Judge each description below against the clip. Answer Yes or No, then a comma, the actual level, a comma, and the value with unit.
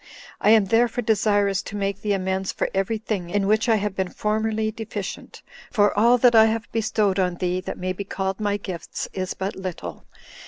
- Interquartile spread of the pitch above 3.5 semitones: No, narrow, 2.4 semitones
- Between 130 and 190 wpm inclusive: No, average, 200 wpm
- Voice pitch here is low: No, high, 205 Hz